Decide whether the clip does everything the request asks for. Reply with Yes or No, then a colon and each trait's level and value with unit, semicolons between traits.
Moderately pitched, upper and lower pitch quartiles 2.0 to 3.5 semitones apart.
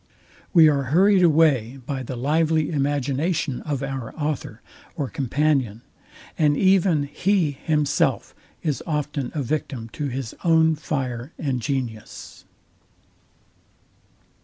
Yes: medium, 145 Hz; average, 3.2 semitones